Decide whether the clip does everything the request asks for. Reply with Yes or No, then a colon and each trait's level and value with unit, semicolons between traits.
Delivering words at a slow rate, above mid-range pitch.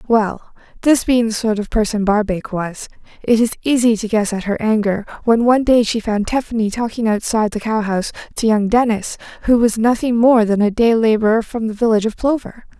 No: average, 200 wpm; high, 220 Hz